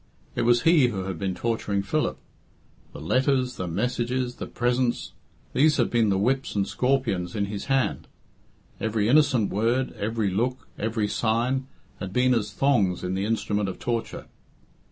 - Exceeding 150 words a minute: Yes, average, 160 wpm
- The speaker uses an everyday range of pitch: Yes, average, 4.0 semitones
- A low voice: Yes, low, 115 Hz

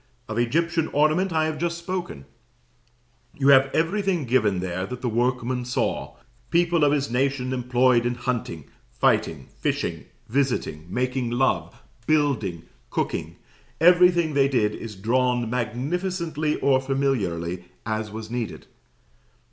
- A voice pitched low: Yes, low, 130 Hz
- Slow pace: Yes, slow, 125 wpm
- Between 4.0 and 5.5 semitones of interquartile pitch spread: Yes, average, 5.2 semitones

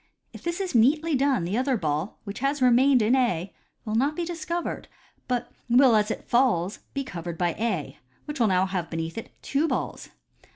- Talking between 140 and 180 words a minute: No, average, 195 wpm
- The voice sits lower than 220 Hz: No, high, 240 Hz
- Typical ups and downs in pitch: No, wide, 6.8 semitones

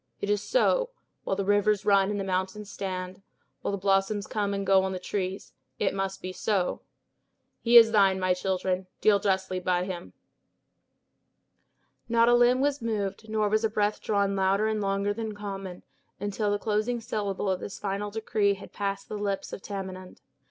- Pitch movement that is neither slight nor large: No, narrow, 1.8 semitones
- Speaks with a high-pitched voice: Yes, high, 200 Hz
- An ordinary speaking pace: Yes, average, 180 wpm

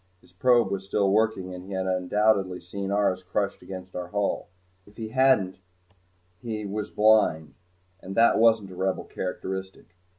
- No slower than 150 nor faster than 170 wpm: Yes, average, 160 wpm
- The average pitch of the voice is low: Yes, very low, 95 Hz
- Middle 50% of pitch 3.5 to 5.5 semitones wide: No, narrow, 2.6 semitones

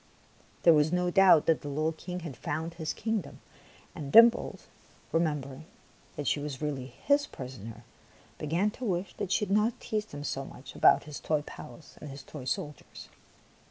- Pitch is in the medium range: Yes, medium, 155 Hz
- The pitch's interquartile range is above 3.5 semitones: Yes, average, 4.3 semitones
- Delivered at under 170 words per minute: No, average, 175 wpm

